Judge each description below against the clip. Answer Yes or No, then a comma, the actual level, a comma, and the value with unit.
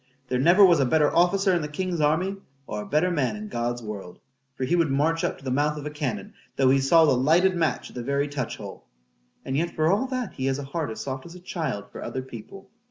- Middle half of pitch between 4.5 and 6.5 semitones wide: Yes, average, 5.0 semitones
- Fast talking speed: Yes, fast, 250 wpm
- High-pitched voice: No, medium, 145 Hz